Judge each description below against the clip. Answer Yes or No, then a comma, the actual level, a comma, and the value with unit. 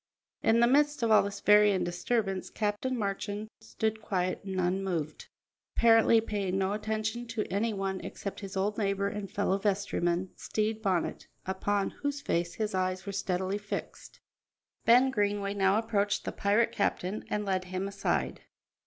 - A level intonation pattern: Yes, narrow, 2.3 semitones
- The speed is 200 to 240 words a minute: No, average, 155 wpm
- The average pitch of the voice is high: Yes, high, 200 Hz